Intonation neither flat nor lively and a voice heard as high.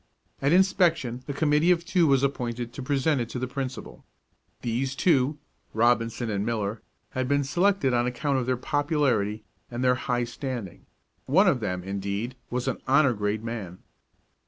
No: average, 3.6 semitones; low, 125 Hz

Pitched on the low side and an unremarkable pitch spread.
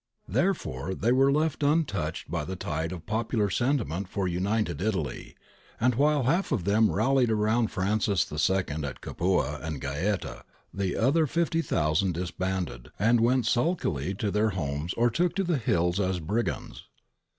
No: low, 100 Hz; wide, 6.2 semitones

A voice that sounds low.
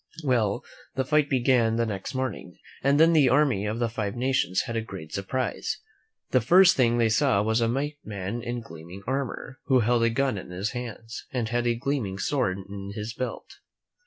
Yes: low, 120 Hz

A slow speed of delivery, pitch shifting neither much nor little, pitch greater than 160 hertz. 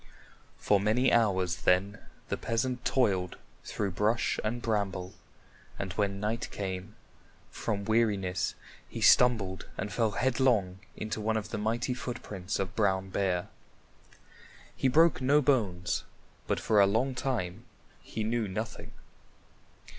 No: slow, 130 wpm; average, 3.7 semitones; low, 105 Hz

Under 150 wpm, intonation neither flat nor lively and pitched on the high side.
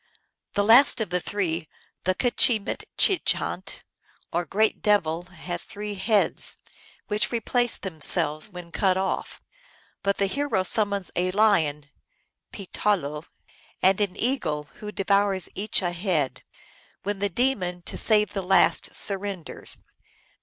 Yes: slow, 135 wpm; average, 3.1 semitones; high, 195 Hz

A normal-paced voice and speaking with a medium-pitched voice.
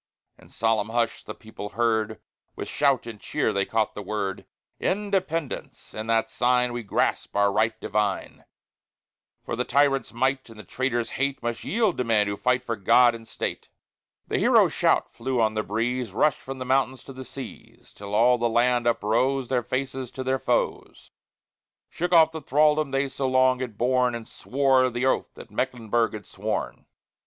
No: average, 180 wpm; low, 125 Hz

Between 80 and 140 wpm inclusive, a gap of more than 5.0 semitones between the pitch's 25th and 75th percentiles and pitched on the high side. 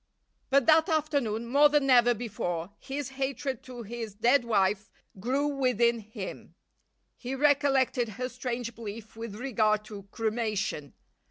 No: slow, 135 wpm; average, 3.9 semitones; high, 240 Hz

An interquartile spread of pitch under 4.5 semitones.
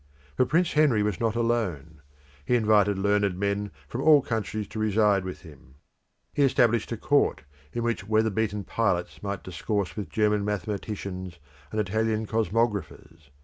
Yes: narrow, 2.4 semitones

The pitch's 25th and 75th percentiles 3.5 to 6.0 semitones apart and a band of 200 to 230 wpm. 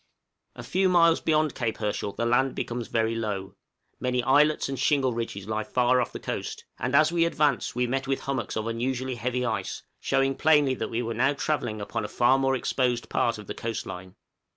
No: average, 3.0 semitones; fast, 205 wpm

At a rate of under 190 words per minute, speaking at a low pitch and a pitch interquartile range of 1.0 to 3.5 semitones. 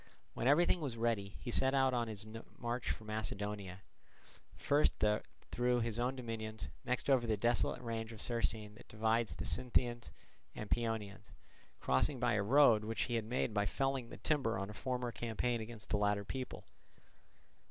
Yes: average, 170 wpm; low, 115 Hz; narrow, 2.6 semitones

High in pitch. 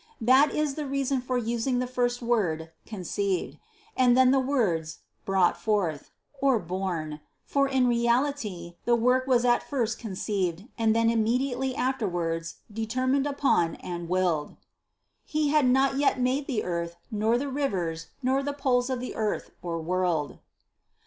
Yes: high, 235 Hz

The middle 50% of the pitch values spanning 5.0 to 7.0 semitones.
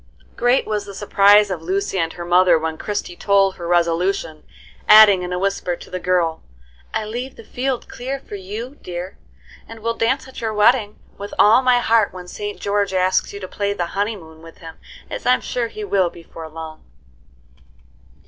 No: average, 3.7 semitones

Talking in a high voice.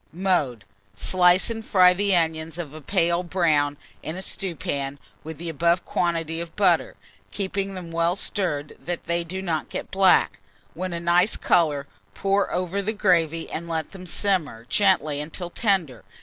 No: medium, 170 Hz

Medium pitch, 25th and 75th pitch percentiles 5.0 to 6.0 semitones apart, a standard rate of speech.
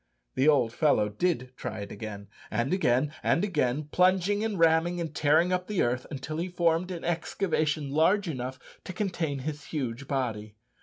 Yes: medium, 155 Hz; wide, 5.6 semitones; average, 170 wpm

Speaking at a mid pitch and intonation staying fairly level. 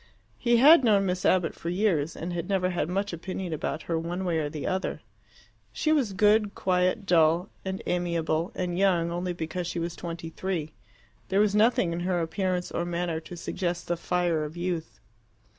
Yes: medium, 180 Hz; narrow, 2.2 semitones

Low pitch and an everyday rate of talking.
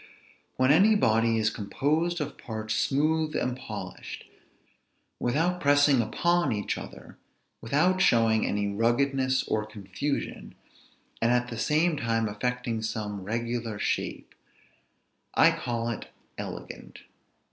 No: low, 120 Hz; slow, 115 wpm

